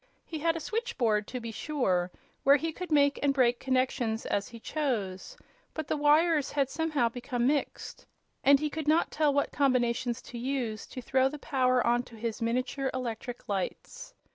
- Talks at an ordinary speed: Yes, average, 180 wpm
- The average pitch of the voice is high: Yes, very high, 260 Hz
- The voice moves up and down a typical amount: Yes, average, 3.9 semitones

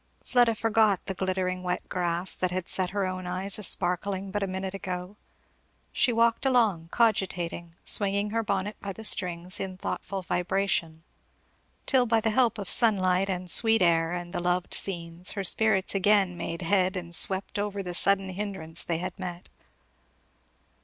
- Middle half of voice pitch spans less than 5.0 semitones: Yes, narrow, 2.4 semitones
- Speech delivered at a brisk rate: No, average, 165 wpm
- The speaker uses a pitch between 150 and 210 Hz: Yes, high, 190 Hz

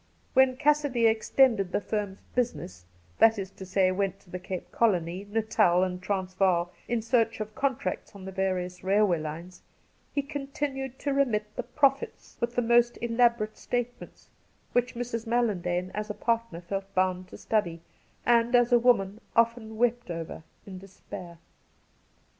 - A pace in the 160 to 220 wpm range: Yes, average, 170 wpm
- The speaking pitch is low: No, high, 215 Hz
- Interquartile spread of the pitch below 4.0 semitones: No, average, 4.5 semitones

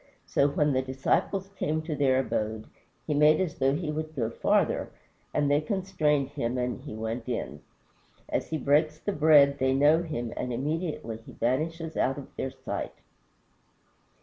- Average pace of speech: Yes, average, 170 wpm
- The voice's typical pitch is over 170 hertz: No, medium, 145 Hz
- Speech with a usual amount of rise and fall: Yes, average, 3.3 semitones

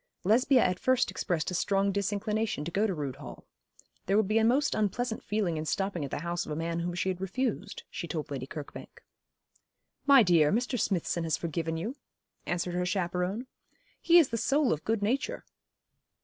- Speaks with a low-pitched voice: No, high, 190 Hz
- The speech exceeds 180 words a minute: Yes, average, 190 wpm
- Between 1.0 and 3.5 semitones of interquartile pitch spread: No, average, 4.8 semitones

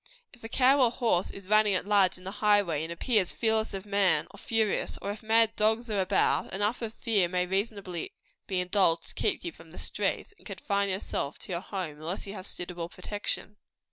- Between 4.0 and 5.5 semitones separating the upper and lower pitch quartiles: No, average, 3.0 semitones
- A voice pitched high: Yes, high, 200 Hz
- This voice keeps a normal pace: No, fast, 210 wpm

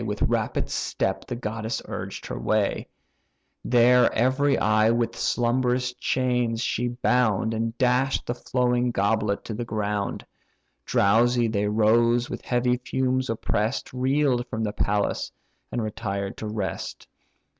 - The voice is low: Yes, low, 120 Hz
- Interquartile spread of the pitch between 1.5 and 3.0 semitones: Yes, narrow, 2.4 semitones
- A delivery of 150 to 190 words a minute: No, slow, 135 wpm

